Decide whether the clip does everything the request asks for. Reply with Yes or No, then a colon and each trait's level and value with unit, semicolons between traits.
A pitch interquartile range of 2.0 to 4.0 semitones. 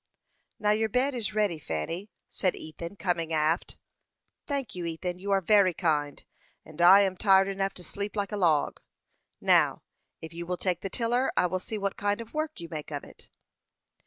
Yes: average, 3.7 semitones